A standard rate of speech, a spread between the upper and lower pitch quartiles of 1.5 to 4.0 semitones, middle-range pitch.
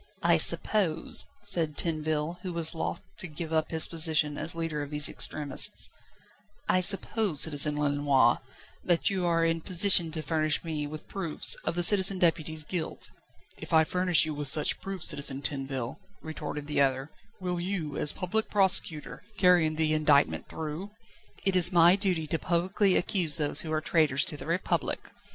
Yes: average, 170 wpm; average, 3.0 semitones; medium, 160 Hz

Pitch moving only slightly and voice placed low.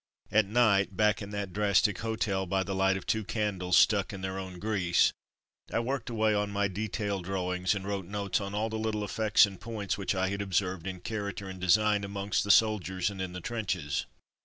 Yes: narrow, 2.0 semitones; low, 100 Hz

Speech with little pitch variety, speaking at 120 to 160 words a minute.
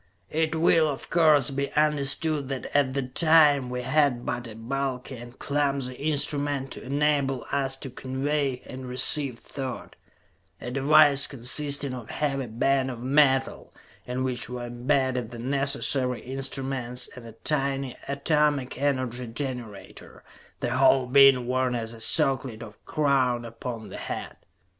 Yes: narrow, 2.2 semitones; average, 145 wpm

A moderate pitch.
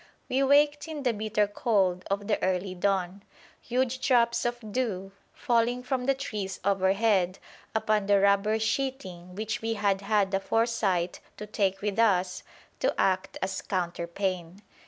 No: high, 205 Hz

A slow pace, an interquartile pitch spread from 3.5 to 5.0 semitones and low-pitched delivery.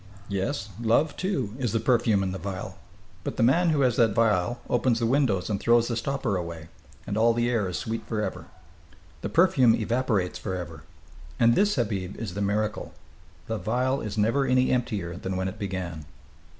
No: average, 185 wpm; average, 4.2 semitones; low, 110 Hz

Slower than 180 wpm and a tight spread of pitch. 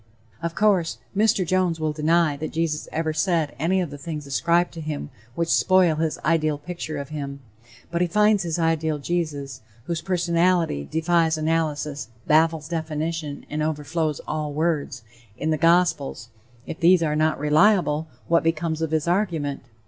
Yes: average, 160 wpm; narrow, 2.1 semitones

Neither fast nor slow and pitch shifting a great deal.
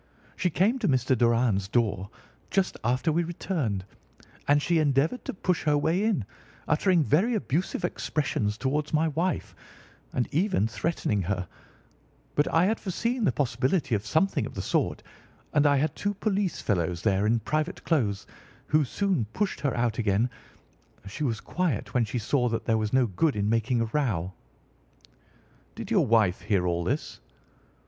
Yes: average, 165 wpm; wide, 7.3 semitones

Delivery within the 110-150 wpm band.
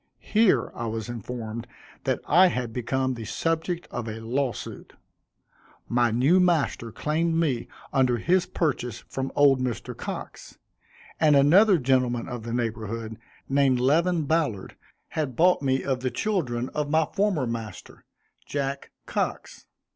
Yes: average, 140 wpm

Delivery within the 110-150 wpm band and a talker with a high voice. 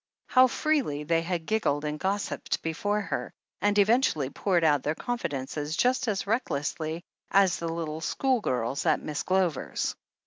No: average, 145 wpm; medium, 170 Hz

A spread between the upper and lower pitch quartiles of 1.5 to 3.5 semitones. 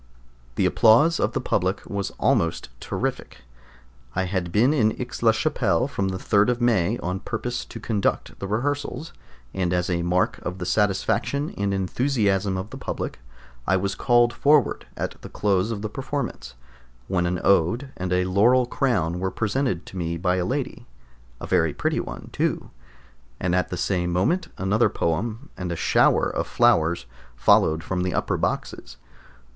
No: average, 4.7 semitones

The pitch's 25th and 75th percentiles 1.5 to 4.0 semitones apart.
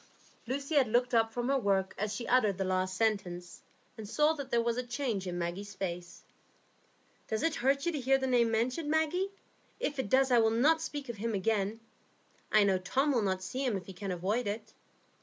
No: average, 5.2 semitones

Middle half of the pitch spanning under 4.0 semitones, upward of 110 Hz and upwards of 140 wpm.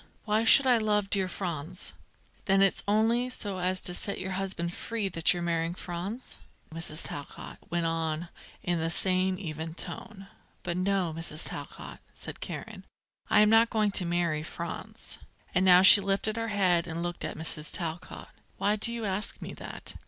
Yes: average, 3.4 semitones; medium, 185 Hz; average, 175 wpm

